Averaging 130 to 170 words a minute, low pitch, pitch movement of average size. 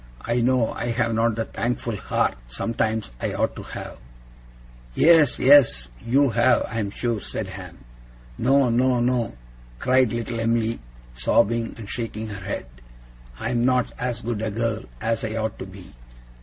No: average, 160 wpm; low, 115 Hz; narrow, 1.9 semitones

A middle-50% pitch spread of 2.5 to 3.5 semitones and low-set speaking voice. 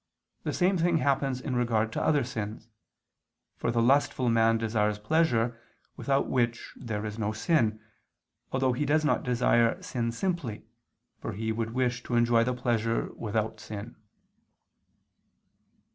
Yes: average, 2.9 semitones; low, 120 Hz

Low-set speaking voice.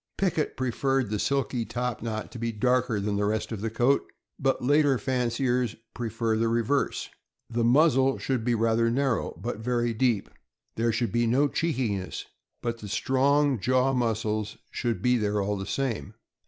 Yes: low, 120 Hz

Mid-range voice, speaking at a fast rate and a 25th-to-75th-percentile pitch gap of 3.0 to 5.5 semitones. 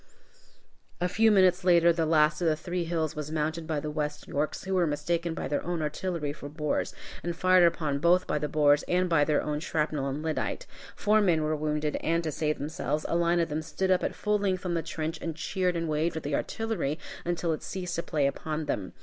No: medium, 160 Hz; fast, 235 wpm; narrow, 2.5 semitones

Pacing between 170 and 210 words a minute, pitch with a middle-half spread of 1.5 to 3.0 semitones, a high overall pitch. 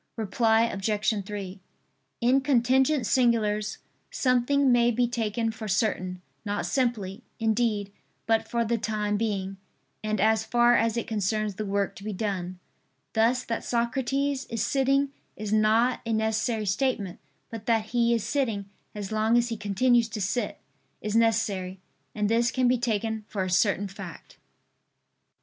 No: average, 150 wpm; narrow, 2.6 semitones; high, 220 Hz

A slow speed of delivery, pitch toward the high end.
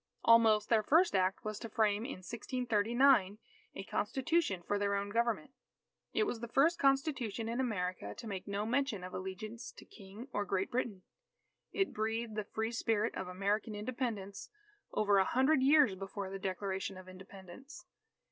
No: average, 165 wpm; high, 215 Hz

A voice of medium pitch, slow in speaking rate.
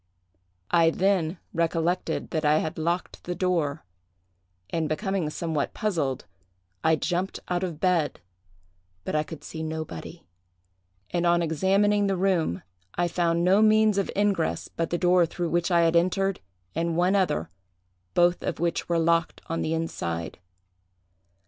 No: medium, 170 Hz; average, 150 wpm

